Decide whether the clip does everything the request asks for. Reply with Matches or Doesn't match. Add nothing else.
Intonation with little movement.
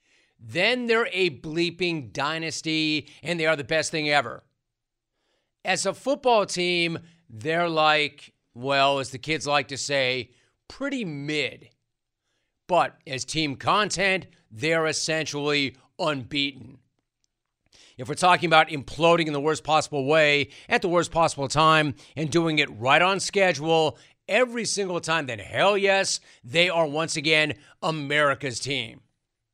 Doesn't match